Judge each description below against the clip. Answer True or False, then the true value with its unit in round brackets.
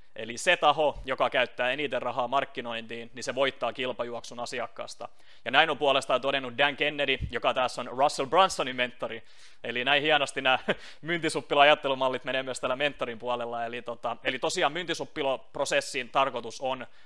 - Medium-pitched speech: False (130 Hz)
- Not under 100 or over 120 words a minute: False (150 wpm)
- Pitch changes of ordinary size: True (3.1 semitones)